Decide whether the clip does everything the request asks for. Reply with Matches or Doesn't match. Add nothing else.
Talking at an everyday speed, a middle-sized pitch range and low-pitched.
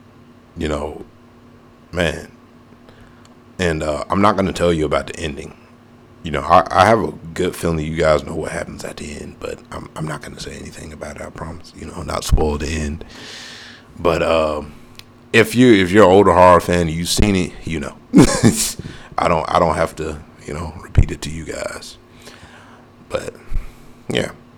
Doesn't match